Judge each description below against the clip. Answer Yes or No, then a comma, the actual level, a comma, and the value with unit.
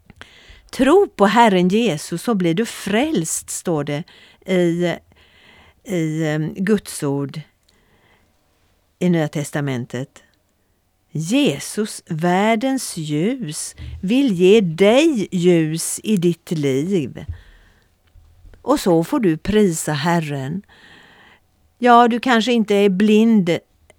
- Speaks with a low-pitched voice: No, medium, 170 Hz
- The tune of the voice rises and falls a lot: Yes, wide, 7.1 semitones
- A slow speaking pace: Yes, slow, 100 wpm